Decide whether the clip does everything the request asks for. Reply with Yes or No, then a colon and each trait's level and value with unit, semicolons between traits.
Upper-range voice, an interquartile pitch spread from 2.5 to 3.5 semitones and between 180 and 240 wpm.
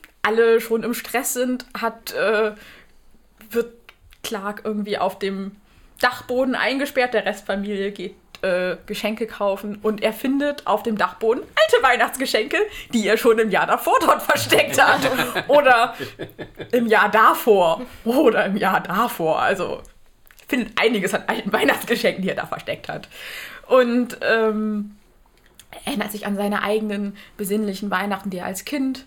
No: high, 220 Hz; average, 3.0 semitones; average, 145 wpm